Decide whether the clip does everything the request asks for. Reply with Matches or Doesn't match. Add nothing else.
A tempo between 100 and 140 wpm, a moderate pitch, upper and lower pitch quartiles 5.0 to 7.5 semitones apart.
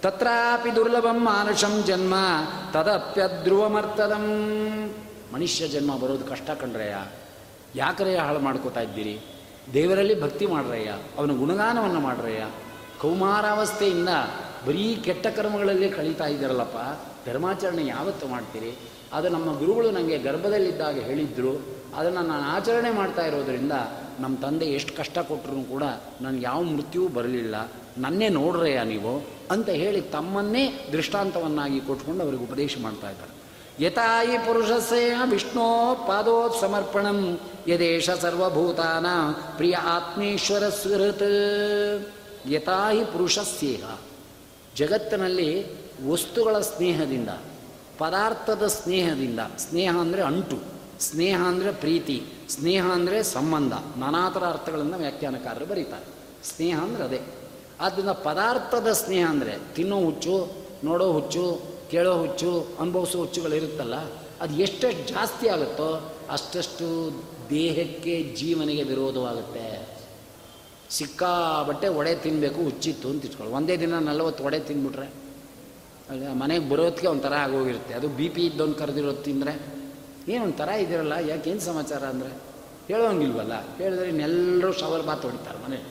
Matches